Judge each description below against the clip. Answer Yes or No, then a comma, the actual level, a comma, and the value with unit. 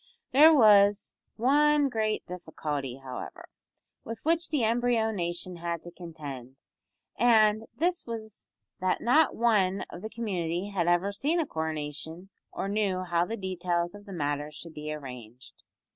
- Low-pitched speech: No, high, 190 Hz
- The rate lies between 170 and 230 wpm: No, average, 145 wpm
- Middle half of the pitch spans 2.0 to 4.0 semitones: No, wide, 5.4 semitones